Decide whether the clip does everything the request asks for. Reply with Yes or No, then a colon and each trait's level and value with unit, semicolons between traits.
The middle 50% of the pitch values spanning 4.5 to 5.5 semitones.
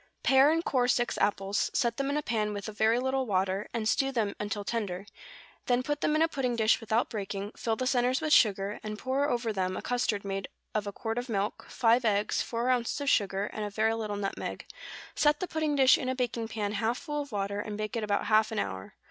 No: average, 3.8 semitones